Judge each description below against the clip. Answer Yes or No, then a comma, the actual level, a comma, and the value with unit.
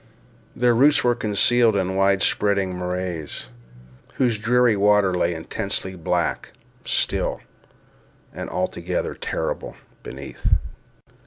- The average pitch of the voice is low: Yes, low, 100 Hz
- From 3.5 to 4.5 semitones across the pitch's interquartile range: Yes, average, 4.0 semitones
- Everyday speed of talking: No, slow, 100 wpm